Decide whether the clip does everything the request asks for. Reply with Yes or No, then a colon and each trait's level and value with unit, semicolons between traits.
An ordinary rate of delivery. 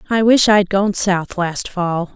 Yes: average, 195 wpm